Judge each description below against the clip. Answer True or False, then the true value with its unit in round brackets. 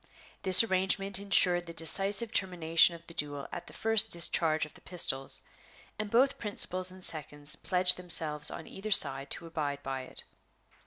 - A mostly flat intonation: False (4.1 semitones)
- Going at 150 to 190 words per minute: True (165 wpm)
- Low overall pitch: False (175 Hz)